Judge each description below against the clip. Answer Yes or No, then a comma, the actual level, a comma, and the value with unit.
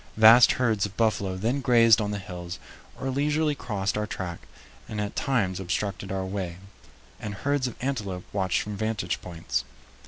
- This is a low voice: Yes, low, 105 Hz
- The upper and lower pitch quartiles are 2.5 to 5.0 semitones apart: Yes, average, 4.1 semitones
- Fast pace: No, average, 165 wpm